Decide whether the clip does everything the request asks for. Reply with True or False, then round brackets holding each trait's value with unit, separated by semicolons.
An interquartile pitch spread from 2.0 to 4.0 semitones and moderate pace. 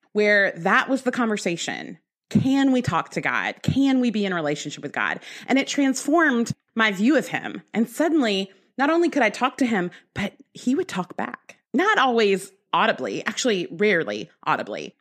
False (5.3 semitones; 180 wpm)